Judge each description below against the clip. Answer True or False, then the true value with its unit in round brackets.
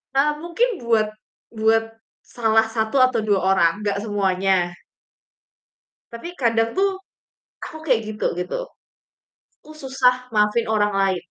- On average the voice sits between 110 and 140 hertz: False (225 Hz)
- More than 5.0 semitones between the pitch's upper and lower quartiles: False (3.3 semitones)